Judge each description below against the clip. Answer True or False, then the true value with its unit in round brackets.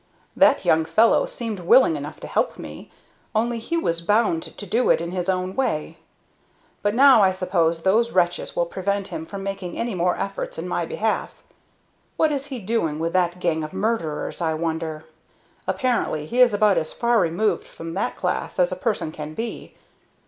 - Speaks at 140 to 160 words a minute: False (185 wpm)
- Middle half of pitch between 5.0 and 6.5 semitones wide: True (5.5 semitones)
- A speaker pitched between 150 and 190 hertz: True (185 Hz)